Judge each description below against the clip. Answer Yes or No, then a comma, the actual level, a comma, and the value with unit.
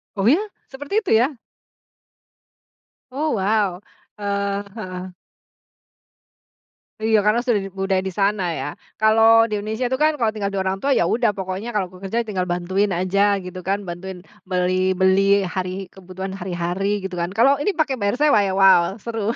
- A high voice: Yes, high, 200 Hz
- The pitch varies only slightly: No, average, 3.2 semitones